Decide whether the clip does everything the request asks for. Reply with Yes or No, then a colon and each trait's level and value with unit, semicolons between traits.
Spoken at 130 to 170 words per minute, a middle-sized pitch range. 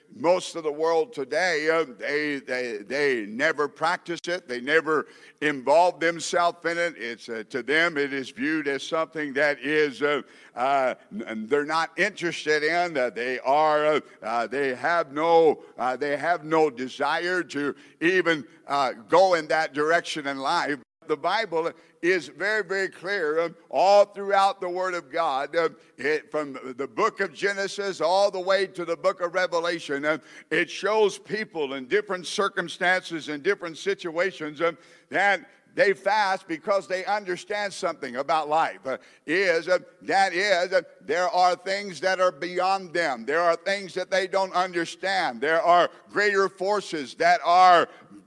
Yes: average, 165 wpm; average, 4.1 semitones